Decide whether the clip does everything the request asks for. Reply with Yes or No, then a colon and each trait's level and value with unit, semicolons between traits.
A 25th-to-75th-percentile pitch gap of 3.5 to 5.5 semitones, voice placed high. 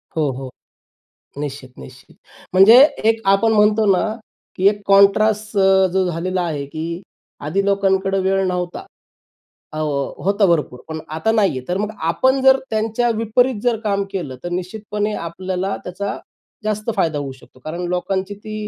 Yes: average, 3.9 semitones; high, 195 Hz